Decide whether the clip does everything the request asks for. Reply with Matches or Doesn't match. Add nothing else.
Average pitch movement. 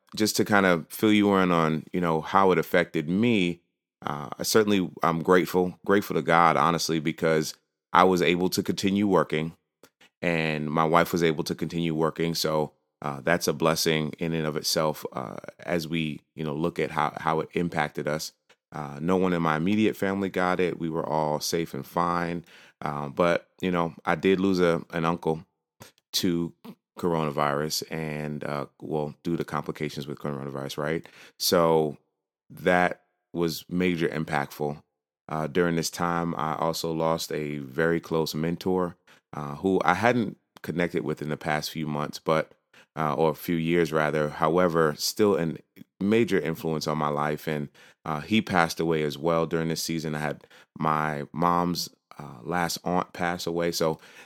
Doesn't match